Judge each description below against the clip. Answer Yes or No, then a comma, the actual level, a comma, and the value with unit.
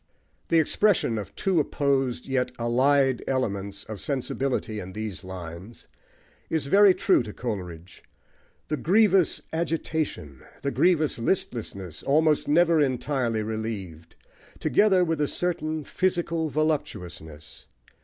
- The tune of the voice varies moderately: No, wide, 7.2 semitones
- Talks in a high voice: No, low, 135 Hz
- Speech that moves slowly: Yes, slow, 115 wpm